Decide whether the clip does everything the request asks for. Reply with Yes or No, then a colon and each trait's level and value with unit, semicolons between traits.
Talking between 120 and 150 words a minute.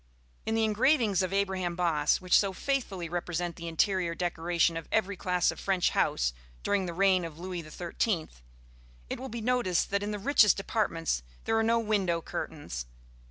No: average, 175 wpm